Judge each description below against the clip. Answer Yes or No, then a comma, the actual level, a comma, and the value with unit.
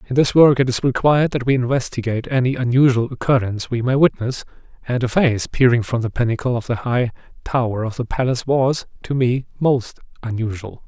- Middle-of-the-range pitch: No, low, 125 Hz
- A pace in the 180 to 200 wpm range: Yes, average, 190 wpm